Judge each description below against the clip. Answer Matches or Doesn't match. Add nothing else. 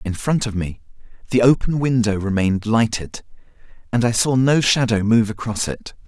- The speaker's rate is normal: Matches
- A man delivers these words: Matches